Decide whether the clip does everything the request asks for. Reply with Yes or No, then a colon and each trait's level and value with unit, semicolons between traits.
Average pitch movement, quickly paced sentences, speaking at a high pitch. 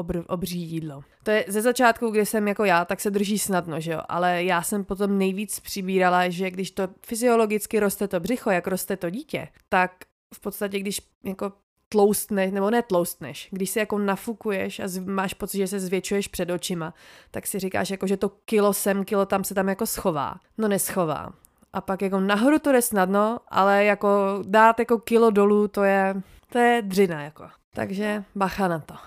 No: narrow, 2.0 semitones; fast, 190 wpm; high, 200 Hz